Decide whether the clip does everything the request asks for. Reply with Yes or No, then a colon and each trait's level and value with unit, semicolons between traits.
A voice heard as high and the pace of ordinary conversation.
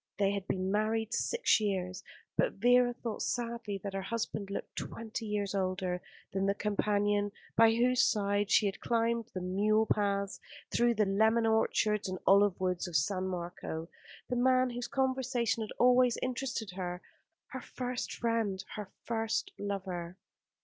Yes: high, 210 Hz; average, 155 wpm